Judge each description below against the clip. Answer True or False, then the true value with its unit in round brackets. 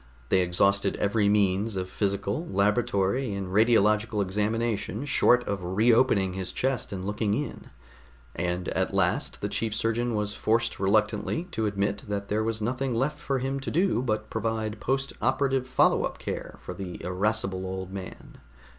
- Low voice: True (105 Hz)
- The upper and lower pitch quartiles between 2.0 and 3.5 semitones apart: True (3.1 semitones)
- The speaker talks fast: False (165 wpm)